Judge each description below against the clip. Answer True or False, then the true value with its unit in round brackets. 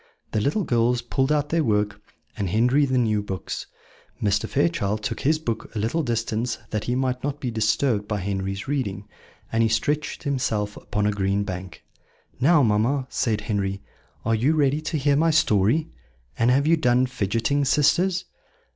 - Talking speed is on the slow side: False (175 wpm)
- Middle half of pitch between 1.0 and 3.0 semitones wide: False (5.3 semitones)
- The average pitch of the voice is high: False (115 Hz)